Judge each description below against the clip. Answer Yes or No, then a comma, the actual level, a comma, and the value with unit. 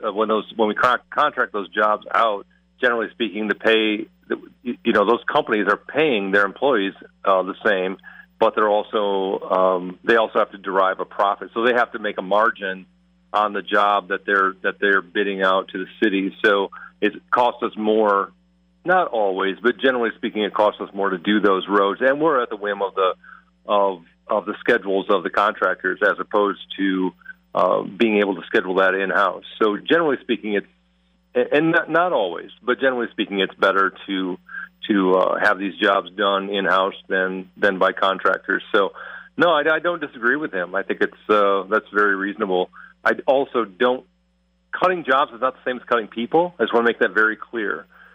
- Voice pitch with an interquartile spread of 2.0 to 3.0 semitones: Yes, narrow, 2.4 semitones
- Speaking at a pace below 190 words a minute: No, average, 195 wpm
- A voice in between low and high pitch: No, low, 100 Hz